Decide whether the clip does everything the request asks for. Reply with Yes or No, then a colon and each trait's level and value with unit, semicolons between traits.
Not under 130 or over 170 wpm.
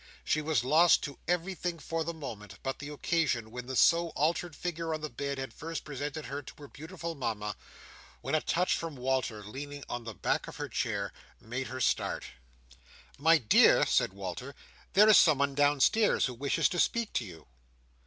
No: average, 185 wpm